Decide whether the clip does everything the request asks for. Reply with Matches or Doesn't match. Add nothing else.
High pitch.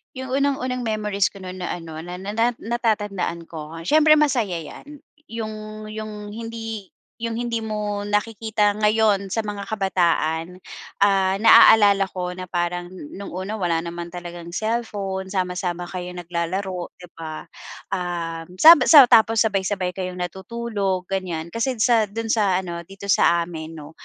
Matches